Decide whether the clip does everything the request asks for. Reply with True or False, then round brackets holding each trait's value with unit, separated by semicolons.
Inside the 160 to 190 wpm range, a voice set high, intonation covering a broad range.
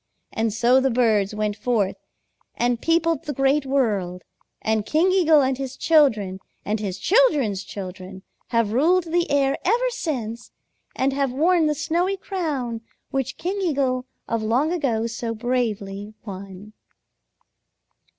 False (140 wpm; 255 Hz; 6.3 semitones)